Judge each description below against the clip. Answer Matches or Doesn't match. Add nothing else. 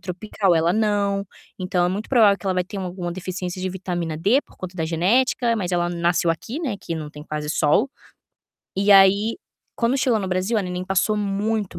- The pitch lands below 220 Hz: Matches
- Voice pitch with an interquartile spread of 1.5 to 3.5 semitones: Matches